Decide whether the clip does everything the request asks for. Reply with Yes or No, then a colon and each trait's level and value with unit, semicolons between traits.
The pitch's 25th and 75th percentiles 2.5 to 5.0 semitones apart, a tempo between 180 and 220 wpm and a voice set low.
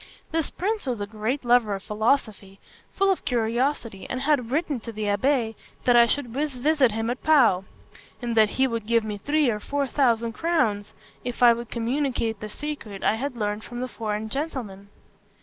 No: average, 4.3 semitones; average, 185 wpm; high, 235 Hz